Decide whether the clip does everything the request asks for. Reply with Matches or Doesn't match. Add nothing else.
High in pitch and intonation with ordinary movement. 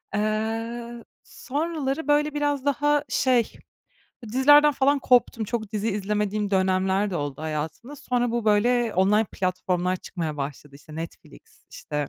Doesn't match